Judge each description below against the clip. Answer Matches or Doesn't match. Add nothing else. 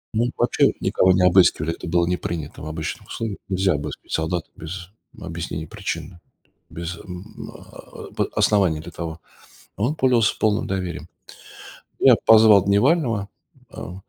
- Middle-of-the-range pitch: Doesn't match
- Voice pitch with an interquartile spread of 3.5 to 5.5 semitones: Matches